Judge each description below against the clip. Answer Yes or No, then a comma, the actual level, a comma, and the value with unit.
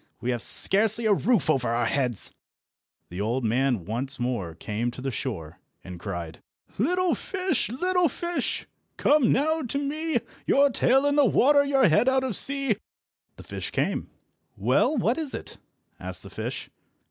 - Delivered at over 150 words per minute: Yes, average, 165 wpm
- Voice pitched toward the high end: Yes, high, 220 Hz